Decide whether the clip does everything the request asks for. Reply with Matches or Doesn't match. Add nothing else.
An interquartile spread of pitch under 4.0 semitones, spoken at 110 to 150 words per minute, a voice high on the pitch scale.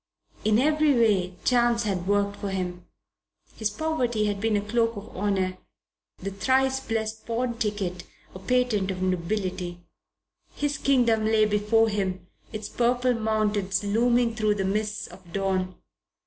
Matches